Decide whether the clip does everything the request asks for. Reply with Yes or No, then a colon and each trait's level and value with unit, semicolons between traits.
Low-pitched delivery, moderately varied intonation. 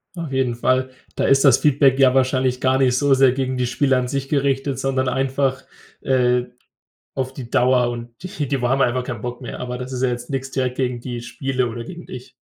No: low, 130 Hz; narrow, 1.5 semitones